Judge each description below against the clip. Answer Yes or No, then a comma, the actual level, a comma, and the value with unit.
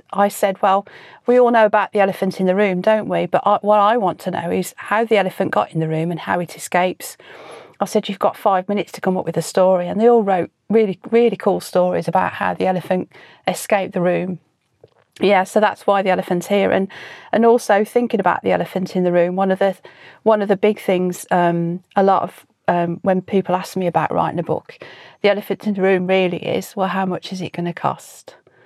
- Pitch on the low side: No, high, 190 Hz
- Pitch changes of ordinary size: No, narrow, 2.3 semitones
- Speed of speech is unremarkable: No, fast, 235 wpm